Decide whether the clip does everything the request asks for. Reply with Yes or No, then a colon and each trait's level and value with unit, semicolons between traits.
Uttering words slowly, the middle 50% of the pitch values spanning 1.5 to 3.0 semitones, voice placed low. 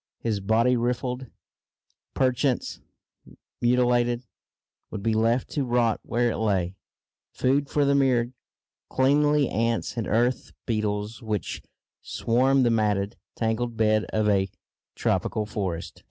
Yes: slow, 120 wpm; average, 2.7 semitones; low, 115 Hz